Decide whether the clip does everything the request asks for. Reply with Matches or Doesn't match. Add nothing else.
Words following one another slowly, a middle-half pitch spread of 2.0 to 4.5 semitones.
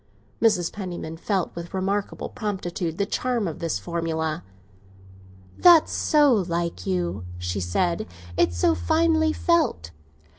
Doesn't match